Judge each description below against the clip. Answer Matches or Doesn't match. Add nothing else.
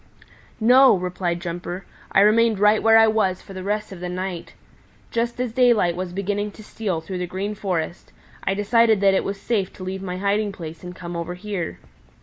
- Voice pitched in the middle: Doesn't match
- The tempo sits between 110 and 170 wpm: Doesn't match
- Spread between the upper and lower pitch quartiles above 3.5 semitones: Doesn't match